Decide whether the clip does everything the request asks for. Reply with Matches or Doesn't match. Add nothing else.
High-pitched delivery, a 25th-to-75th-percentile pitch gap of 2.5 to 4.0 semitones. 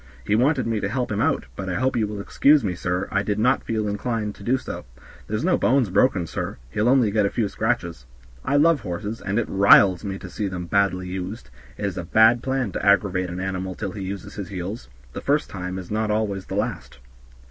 Doesn't match